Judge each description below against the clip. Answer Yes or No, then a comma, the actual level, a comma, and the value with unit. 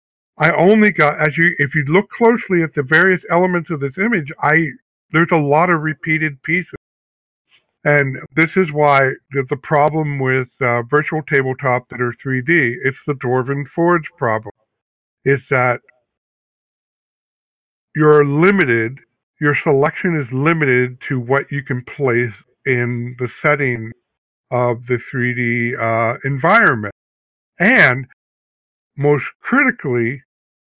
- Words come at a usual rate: No, slow, 125 wpm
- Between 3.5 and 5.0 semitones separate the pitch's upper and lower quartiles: Yes, average, 4.3 semitones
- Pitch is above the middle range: No, medium, 140 Hz